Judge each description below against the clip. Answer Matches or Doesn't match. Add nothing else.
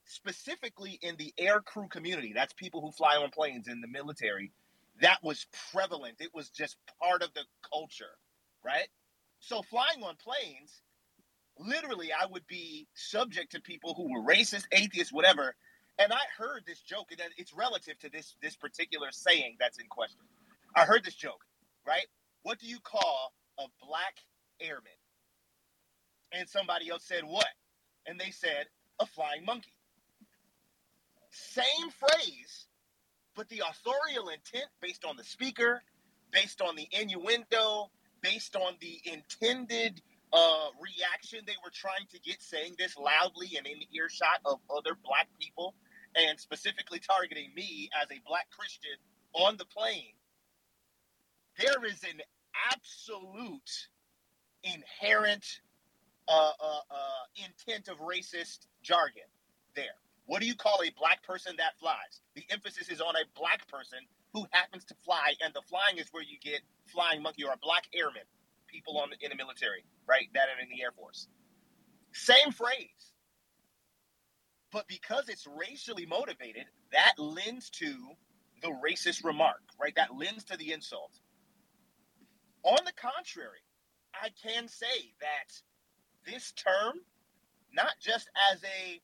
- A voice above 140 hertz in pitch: Matches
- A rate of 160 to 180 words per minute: Doesn't match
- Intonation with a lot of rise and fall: Matches